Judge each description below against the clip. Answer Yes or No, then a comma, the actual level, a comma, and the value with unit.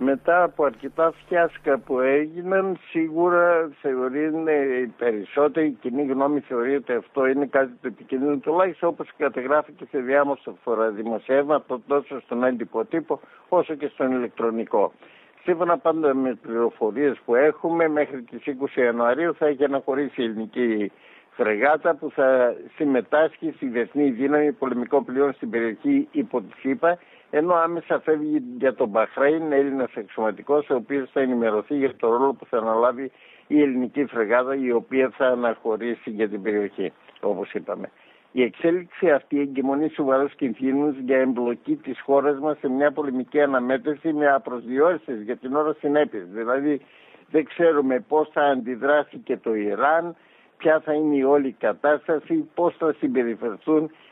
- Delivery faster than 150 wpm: No, average, 145 wpm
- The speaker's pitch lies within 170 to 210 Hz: No, medium, 140 Hz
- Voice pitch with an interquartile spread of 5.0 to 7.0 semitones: No, average, 3.2 semitones